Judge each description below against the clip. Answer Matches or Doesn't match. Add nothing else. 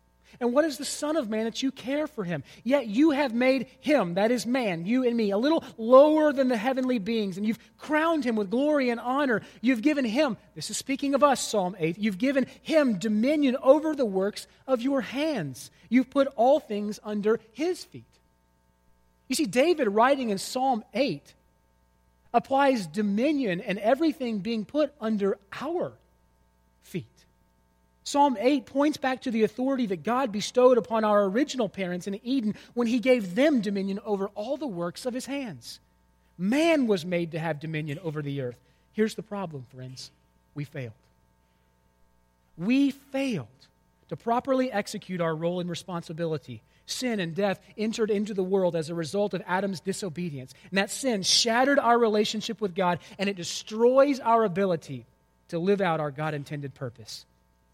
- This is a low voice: Doesn't match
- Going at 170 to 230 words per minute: Matches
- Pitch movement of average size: Doesn't match